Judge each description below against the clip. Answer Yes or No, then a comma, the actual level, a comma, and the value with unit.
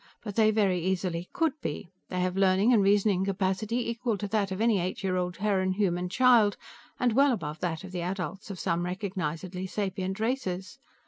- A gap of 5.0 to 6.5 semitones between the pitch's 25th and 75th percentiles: No, average, 2.9 semitones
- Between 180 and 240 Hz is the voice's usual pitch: Yes, high, 190 Hz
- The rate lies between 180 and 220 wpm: Yes, average, 190 wpm